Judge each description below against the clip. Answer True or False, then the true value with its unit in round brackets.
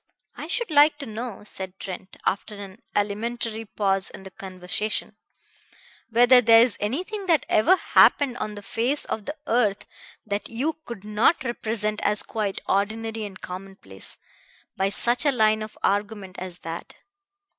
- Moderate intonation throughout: True (3.4 semitones)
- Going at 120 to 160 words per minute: True (155 wpm)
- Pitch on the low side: False (215 Hz)